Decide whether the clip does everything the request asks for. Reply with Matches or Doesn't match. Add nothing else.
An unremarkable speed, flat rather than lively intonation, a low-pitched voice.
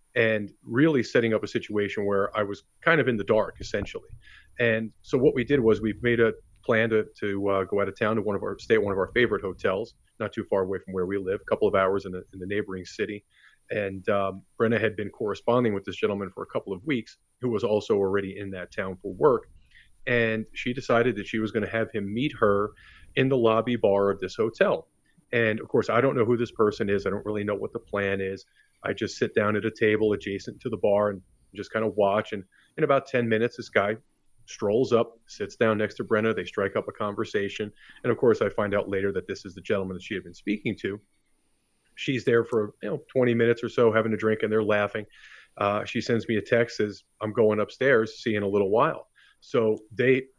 Doesn't match